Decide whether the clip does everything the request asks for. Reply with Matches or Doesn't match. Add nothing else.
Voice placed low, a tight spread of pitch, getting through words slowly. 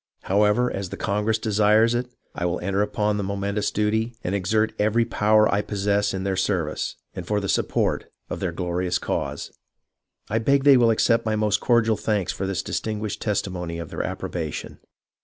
Doesn't match